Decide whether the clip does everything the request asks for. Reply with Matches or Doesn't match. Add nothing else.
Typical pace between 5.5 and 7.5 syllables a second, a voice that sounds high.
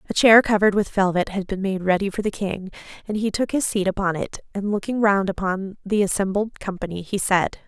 Matches